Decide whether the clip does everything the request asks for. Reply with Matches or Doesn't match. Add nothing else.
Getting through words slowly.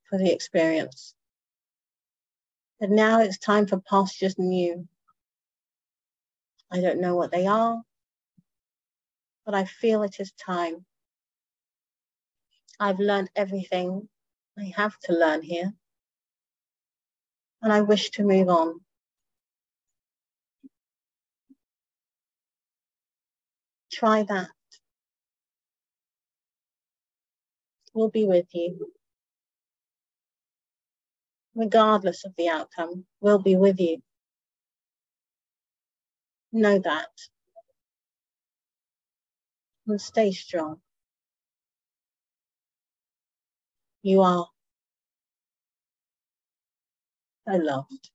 Matches